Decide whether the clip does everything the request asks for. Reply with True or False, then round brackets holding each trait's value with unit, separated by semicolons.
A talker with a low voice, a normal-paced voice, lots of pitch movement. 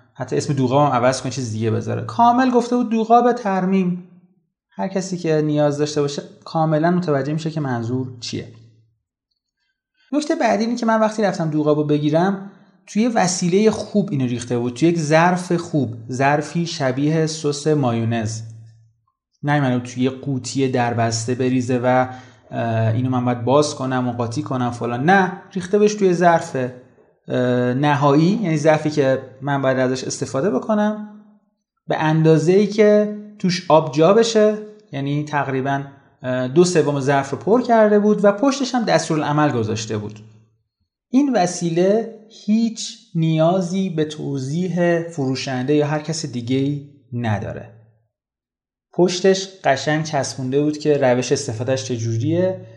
False (150 Hz; 145 wpm; 6.8 semitones)